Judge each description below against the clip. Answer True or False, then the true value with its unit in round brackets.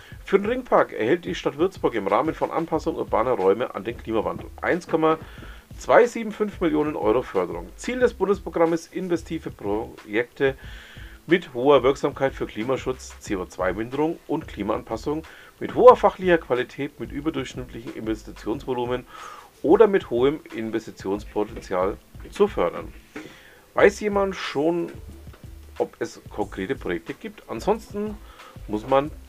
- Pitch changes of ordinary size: False (8.9 semitones)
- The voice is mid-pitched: True (150 Hz)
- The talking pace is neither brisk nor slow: False (115 wpm)